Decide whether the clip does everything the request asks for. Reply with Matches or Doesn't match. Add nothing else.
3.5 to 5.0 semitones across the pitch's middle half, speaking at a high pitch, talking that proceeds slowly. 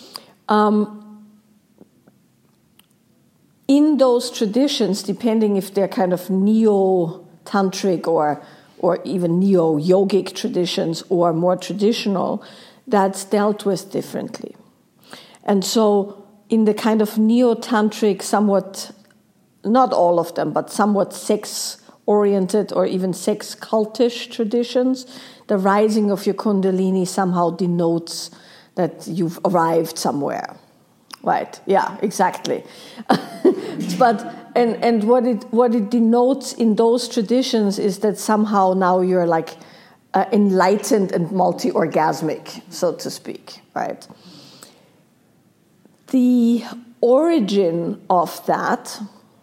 Matches